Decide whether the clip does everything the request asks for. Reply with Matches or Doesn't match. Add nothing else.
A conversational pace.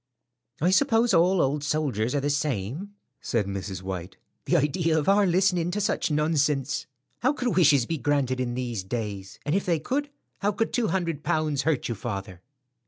Matches